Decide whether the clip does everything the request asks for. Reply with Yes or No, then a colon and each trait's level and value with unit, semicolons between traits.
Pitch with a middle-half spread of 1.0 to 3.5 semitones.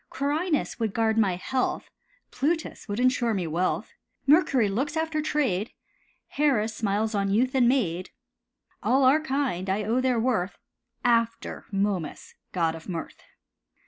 No: wide, 5.4 semitones